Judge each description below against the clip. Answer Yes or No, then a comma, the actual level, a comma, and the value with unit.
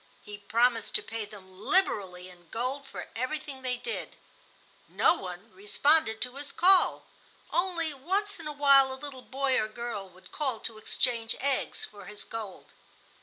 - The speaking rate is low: No, average, 155 wpm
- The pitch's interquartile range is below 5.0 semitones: No, wide, 5.5 semitones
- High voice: Yes, very high, 250 Hz